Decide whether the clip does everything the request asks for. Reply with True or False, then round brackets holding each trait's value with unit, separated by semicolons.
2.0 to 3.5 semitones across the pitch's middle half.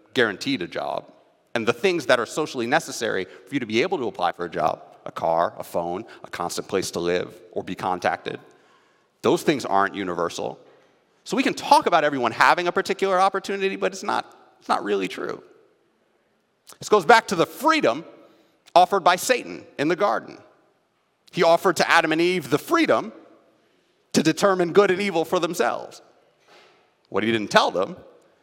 False (4.2 semitones)